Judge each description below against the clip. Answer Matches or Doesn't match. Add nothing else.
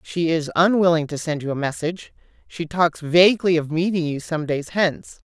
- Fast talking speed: Doesn't match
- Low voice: Doesn't match